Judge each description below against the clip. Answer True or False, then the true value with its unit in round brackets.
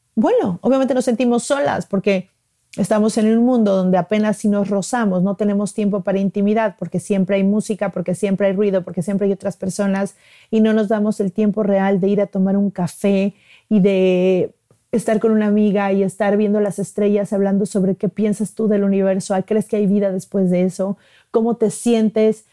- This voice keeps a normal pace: False (195 wpm)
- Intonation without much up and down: True (1.8 semitones)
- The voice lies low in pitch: False (205 Hz)